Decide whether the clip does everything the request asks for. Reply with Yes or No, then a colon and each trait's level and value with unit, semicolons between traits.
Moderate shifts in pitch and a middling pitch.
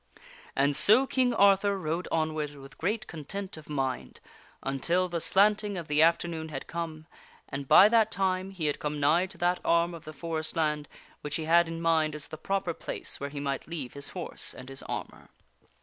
Yes: average, 3.7 semitones; medium, 165 Hz